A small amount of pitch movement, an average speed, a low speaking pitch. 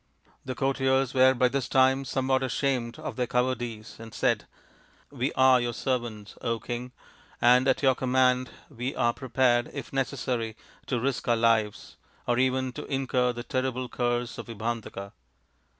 Yes: narrow, 1.7 semitones; average, 165 wpm; low, 125 Hz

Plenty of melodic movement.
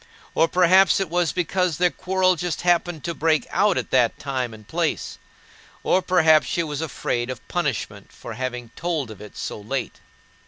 Yes: wide, 5.8 semitones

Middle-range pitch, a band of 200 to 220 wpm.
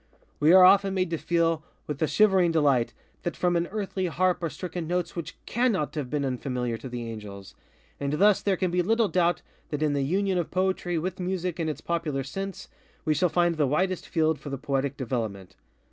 Yes: medium, 170 Hz; fast, 205 wpm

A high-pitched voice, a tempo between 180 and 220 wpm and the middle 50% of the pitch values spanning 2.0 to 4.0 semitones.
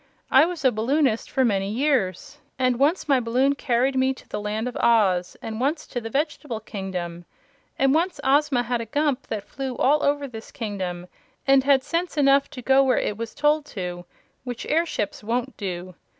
No: very high, 255 Hz; average, 190 wpm; average, 4.5 semitones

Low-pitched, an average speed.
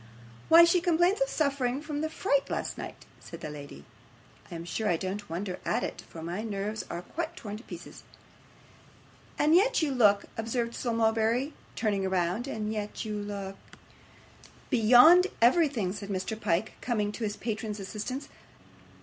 No: high, 220 Hz; average, 170 wpm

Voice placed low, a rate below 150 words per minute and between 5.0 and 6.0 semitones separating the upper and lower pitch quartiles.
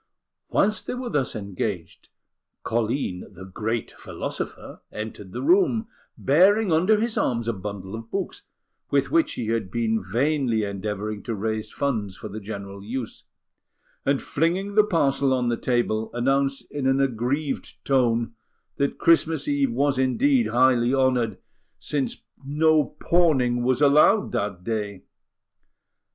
Yes: low, 125 Hz; average, 140 wpm; average, 5.3 semitones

